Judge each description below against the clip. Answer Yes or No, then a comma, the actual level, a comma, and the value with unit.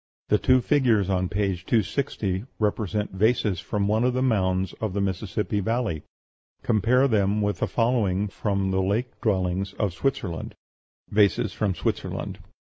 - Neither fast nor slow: Yes, average, 145 wpm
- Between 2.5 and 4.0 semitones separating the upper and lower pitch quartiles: Yes, average, 3.1 semitones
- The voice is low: Yes, low, 105 Hz